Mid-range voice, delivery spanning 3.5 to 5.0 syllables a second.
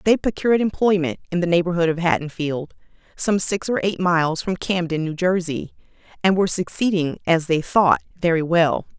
No: medium, 175 Hz; 5.4 syllables/s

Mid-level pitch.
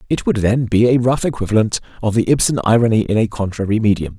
No: low, 110 Hz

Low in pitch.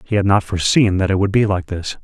Yes: low, 100 Hz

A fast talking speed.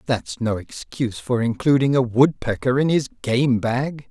No: average, 160 wpm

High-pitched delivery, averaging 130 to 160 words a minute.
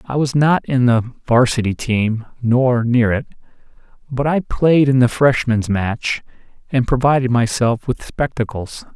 No: low, 125 Hz; average, 145 wpm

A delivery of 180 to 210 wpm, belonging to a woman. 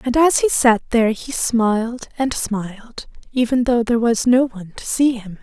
Yes: average, 200 wpm; female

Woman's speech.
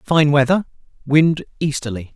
No: male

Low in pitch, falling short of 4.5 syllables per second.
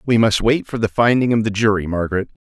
No: low, 110 Hz; 6.3 syllables/s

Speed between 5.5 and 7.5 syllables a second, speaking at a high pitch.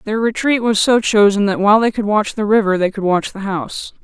Yes: 5.7 syllables/s; high, 210 Hz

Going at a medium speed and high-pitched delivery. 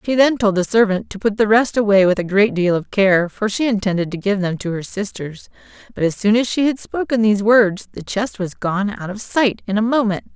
No: fast, 255 wpm; high, 210 Hz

